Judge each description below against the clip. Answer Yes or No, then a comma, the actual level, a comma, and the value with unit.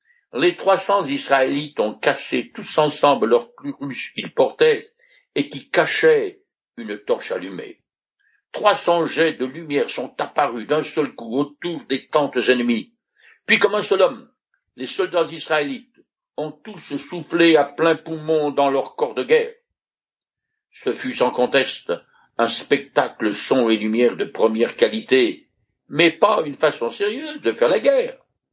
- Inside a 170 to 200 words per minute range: No, average, 150 wpm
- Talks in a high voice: No, medium, 170 Hz